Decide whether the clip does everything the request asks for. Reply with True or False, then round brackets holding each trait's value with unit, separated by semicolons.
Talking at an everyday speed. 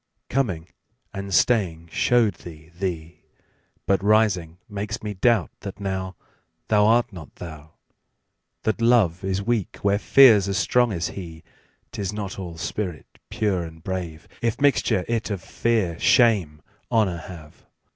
False (125 wpm)